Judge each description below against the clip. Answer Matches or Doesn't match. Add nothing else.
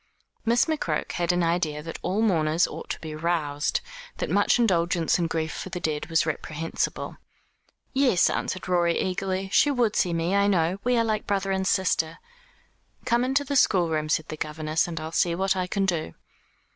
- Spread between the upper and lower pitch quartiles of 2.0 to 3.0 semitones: Doesn't match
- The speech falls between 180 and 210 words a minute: Matches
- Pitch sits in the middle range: Matches